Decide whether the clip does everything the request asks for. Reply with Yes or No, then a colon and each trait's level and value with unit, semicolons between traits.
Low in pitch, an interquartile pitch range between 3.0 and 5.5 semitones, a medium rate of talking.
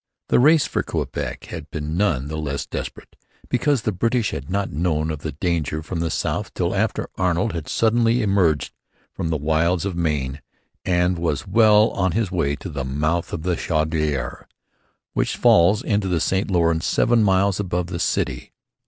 Yes: very low, 85 Hz; average, 4.3 semitones; average, 180 wpm